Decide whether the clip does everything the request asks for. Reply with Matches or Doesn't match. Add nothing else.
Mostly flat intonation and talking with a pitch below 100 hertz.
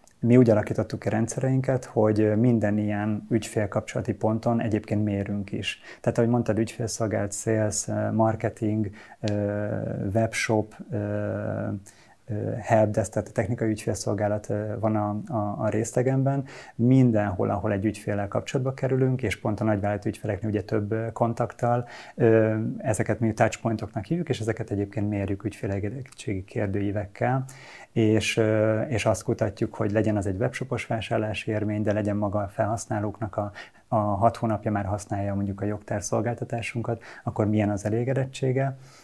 Doesn't match